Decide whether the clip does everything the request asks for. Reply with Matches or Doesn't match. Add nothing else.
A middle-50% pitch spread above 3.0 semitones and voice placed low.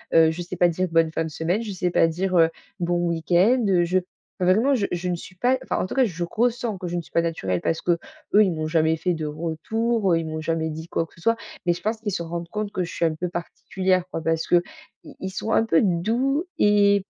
Doesn't match